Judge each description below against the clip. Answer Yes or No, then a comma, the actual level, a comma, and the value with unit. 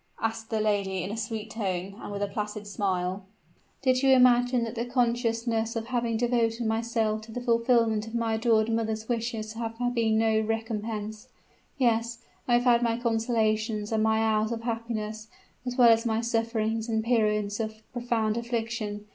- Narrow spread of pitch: Yes, narrow, 1.4 semitones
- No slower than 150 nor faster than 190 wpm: Yes, average, 170 wpm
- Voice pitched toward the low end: No, high, 225 Hz